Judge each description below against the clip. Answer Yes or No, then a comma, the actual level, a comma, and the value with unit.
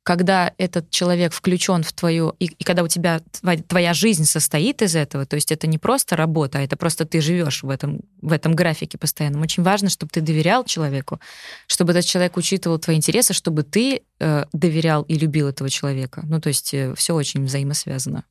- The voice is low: No, medium, 165 Hz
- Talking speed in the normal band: No, fast, 195 wpm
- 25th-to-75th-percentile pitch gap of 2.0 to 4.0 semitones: Yes, average, 2.7 semitones